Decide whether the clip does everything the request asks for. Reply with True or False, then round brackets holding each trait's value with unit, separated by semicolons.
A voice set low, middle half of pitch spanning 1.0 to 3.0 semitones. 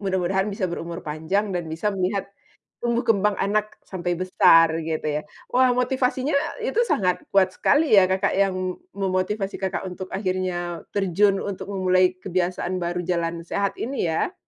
False (190 Hz; 2.5 semitones)